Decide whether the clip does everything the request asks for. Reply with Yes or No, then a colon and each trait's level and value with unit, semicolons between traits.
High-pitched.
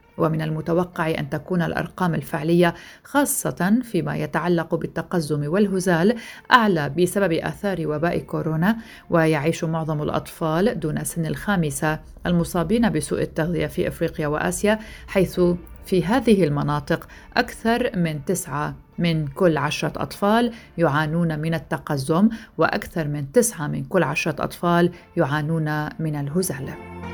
No: medium, 165 Hz